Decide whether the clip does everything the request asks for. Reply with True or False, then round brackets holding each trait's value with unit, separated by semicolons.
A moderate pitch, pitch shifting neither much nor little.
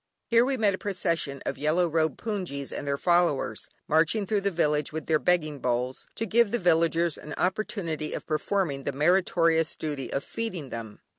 True (165 Hz; 4.3 semitones)